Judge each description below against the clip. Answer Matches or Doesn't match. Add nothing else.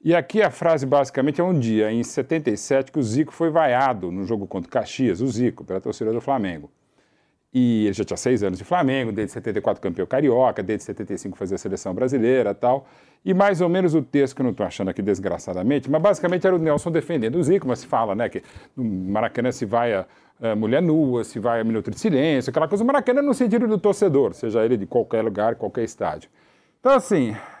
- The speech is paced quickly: Matches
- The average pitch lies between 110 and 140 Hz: Matches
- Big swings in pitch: Matches